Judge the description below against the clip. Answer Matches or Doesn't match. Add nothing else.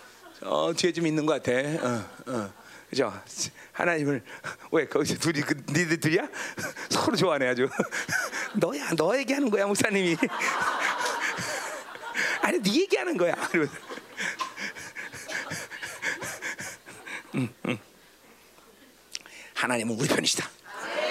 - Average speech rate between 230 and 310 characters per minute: Doesn't match